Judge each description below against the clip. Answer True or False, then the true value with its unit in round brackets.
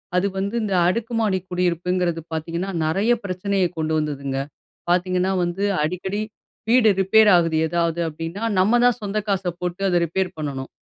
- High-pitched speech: False (180 Hz)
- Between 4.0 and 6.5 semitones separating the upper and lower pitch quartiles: False (3.0 semitones)